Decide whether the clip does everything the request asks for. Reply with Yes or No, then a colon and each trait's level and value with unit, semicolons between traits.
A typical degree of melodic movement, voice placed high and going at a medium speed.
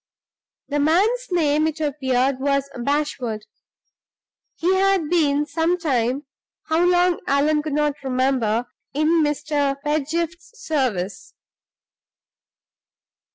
No: average, 3.3 semitones; very high, 295 Hz; slow, 100 wpm